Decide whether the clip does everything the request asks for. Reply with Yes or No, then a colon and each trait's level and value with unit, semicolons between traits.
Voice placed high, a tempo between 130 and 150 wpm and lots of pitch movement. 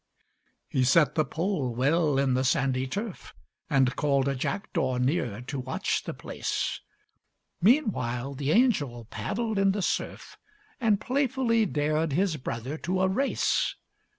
No: medium, 150 Hz; average, 140 wpm; wide, 7.3 semitones